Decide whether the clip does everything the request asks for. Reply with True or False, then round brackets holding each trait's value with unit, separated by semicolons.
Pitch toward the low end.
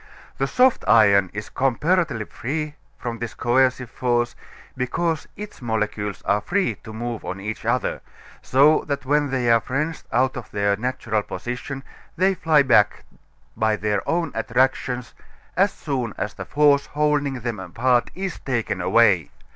True (125 Hz)